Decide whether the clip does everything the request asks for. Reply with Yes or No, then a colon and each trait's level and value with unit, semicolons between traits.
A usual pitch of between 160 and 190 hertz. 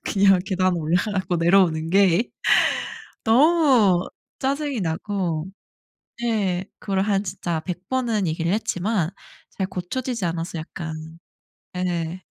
Yes: medium, 185 Hz